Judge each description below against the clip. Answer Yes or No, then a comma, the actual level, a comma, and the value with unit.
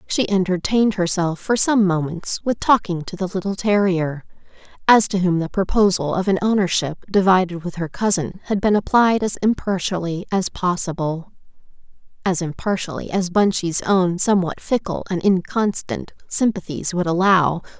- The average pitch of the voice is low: No, medium, 185 Hz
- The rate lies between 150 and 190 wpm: No, average, 140 wpm